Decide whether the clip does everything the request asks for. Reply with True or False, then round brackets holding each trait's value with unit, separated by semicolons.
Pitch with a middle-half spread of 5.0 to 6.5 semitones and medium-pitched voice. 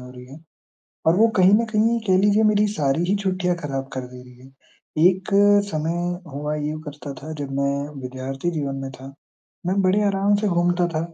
True (5.4 semitones; 160 Hz)